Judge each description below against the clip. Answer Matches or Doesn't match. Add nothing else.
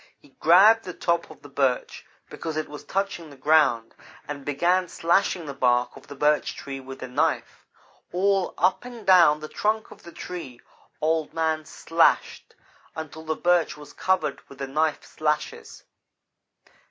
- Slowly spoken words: Doesn't match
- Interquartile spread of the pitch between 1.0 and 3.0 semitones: Doesn't match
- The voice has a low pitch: Doesn't match